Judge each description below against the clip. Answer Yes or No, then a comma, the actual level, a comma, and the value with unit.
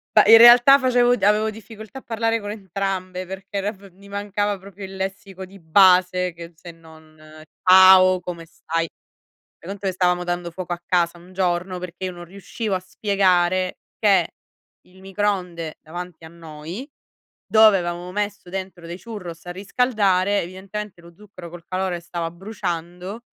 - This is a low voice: No, medium, 185 Hz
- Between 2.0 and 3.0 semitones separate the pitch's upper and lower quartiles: Yes, narrow, 2.6 semitones